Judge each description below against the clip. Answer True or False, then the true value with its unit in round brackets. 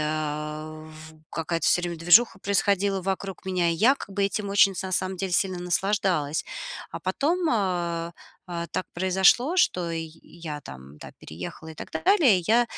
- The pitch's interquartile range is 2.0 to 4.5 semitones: True (3.7 semitones)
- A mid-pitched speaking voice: True (180 Hz)